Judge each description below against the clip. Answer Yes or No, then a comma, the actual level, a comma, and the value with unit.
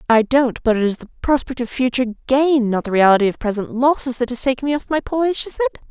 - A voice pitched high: Yes, very high, 255 Hz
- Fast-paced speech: Yes, fast, 245 wpm